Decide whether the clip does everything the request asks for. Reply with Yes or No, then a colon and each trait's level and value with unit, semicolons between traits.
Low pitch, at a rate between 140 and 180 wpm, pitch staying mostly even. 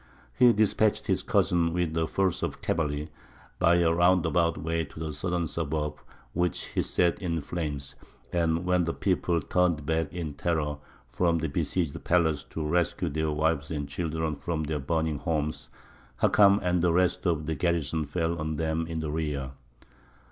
Yes: very low, 80 Hz; average, 170 wpm; narrow, 2.2 semitones